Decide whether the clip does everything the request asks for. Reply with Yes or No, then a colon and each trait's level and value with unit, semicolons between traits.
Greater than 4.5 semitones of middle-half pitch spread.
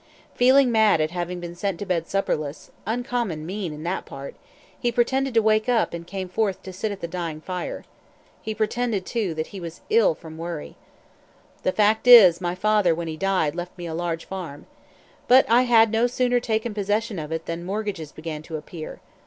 Yes: average, 4.9 semitones